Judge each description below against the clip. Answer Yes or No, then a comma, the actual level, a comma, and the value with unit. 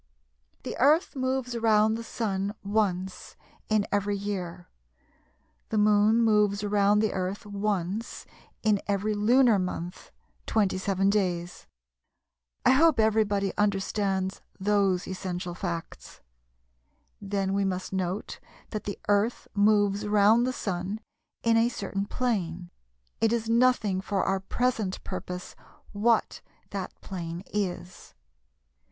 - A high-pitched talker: Yes, high, 205 Hz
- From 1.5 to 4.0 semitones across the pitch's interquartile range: Yes, narrow, 2.4 semitones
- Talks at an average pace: No, slow, 115 wpm